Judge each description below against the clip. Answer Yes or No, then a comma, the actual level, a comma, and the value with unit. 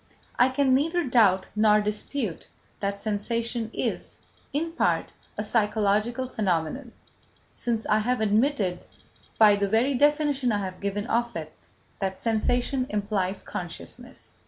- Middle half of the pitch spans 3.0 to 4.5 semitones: Yes, average, 3.8 semitones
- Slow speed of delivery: Yes, slow, 130 wpm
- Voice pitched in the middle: No, high, 220 Hz